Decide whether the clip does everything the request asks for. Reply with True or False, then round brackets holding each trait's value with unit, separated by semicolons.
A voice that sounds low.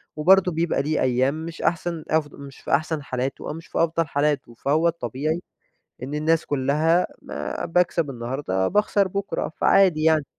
False (155 Hz)